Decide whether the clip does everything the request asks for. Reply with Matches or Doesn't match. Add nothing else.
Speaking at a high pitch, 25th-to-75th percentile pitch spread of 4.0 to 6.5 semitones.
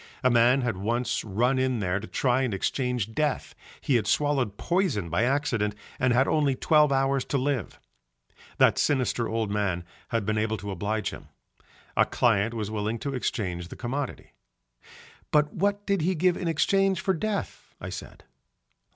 Doesn't match